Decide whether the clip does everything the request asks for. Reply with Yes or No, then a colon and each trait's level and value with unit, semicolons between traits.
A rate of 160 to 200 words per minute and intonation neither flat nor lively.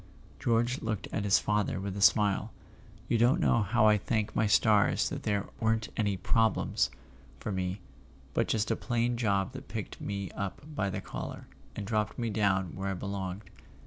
No: average, 180 wpm; narrow, 2.3 semitones